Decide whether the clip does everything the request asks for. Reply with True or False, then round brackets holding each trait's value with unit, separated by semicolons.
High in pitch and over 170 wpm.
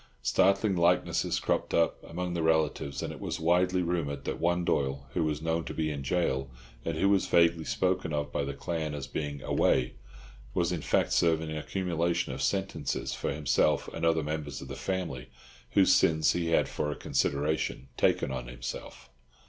False (80 Hz; 185 wpm)